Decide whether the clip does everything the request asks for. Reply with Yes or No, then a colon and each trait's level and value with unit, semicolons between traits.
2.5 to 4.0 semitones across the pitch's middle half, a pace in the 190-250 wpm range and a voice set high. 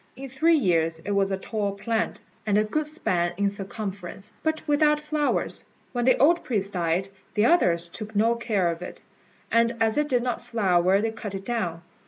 No: average, 4.6 semitones; average, 195 wpm; high, 215 Hz